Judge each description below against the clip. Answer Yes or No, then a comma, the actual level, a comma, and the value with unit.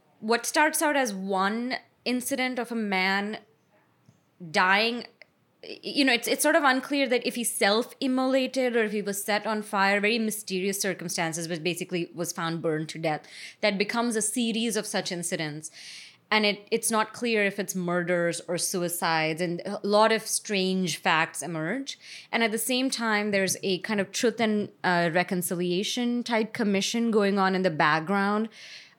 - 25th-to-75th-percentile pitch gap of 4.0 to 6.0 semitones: Yes, average, 4.5 semitones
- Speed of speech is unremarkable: Yes, average, 170 wpm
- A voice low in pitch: No, high, 205 Hz